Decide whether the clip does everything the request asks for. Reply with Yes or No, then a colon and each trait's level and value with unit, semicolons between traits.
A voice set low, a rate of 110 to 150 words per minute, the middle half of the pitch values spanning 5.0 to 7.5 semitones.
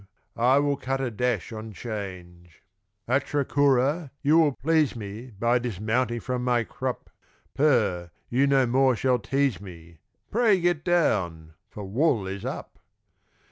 Yes: low, 125 Hz; average, 140 wpm; average, 5.3 semitones